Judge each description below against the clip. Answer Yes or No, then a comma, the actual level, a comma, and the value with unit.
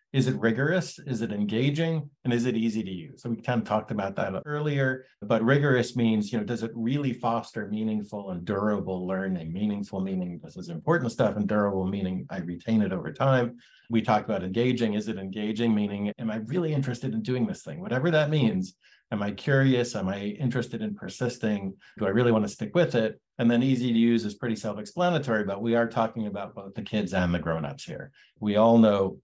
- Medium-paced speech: No, fast, 215 wpm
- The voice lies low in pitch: Yes, low, 115 Hz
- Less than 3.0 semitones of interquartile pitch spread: No, average, 3.6 semitones